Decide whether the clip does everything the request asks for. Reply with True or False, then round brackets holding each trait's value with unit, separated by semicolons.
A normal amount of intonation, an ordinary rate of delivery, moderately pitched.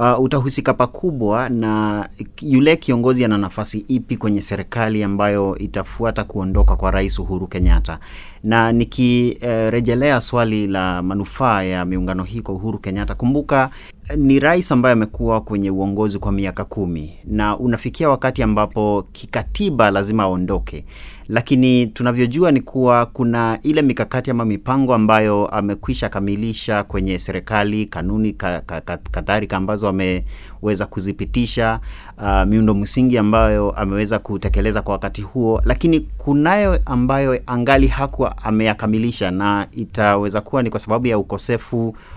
False (3.7 semitones; 130 wpm; 110 Hz)